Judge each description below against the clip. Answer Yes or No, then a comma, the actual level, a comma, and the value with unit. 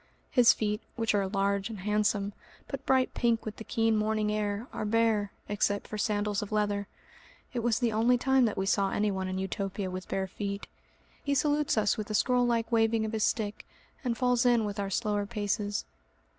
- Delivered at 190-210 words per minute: Yes, average, 200 wpm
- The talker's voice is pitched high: Yes, high, 215 Hz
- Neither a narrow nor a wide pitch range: No, narrow, 2.3 semitones